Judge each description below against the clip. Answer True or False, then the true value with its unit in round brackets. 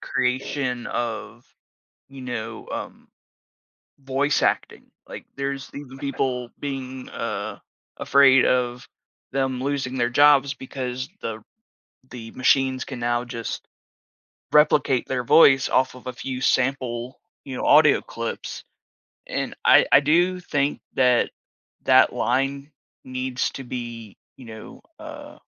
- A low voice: True (130 Hz)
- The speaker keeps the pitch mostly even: True (2.0 semitones)